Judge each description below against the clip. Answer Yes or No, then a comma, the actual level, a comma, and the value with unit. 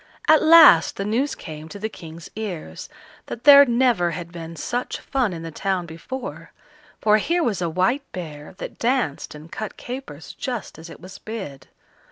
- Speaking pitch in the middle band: No, high, 195 Hz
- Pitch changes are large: Yes, wide, 7.0 semitones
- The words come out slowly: No, average, 180 wpm